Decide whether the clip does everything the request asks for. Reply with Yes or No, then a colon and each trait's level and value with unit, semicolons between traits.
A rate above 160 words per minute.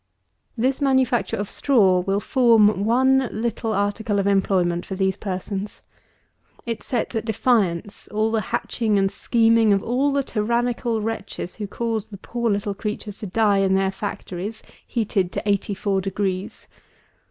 No: average, 155 wpm